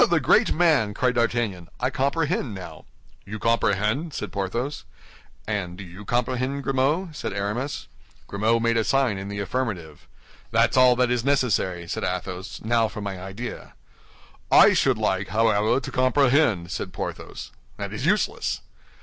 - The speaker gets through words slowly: No, average, 155 wpm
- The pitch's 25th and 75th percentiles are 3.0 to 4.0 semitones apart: No, average, 4.6 semitones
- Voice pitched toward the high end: No, low, 115 Hz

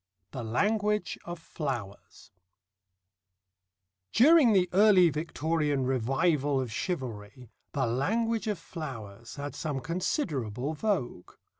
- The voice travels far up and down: Yes, wide, 6.8 semitones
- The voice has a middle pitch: Yes, medium, 150 Hz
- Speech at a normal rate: No, slow, 100 wpm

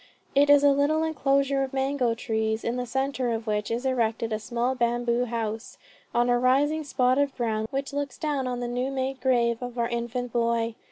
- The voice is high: Yes, high, 245 Hz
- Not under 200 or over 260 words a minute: Yes, fast, 205 wpm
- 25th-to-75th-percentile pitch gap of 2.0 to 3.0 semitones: Yes, narrow, 2.6 semitones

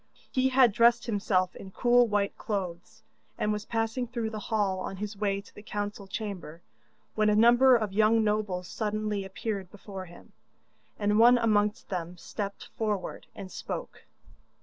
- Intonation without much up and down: Yes, narrow, 2.3 semitones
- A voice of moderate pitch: No, high, 210 Hz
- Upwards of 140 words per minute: Yes, average, 160 wpm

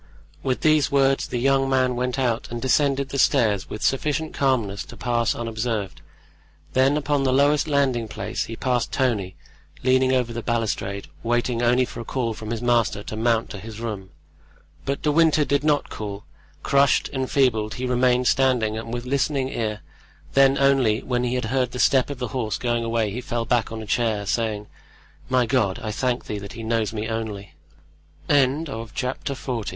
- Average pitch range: Yes, average, 3.1 semitones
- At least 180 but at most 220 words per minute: Yes, average, 185 wpm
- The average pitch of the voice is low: Yes, low, 120 Hz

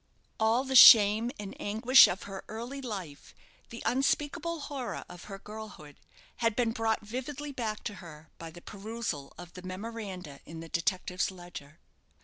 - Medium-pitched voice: No, high, 210 Hz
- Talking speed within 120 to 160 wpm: Yes, average, 155 wpm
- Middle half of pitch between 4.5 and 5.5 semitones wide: Yes, average, 4.9 semitones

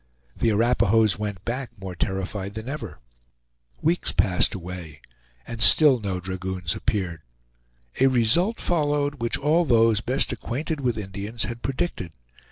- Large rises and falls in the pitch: Yes, wide, 5.9 semitones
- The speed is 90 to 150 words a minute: Yes, slow, 135 wpm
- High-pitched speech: No, low, 115 Hz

